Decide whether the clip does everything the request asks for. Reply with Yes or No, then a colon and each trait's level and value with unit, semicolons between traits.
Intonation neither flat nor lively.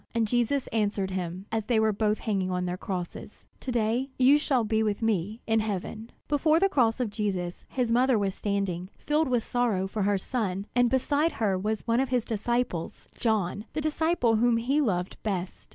Yes: average, 3.9 semitones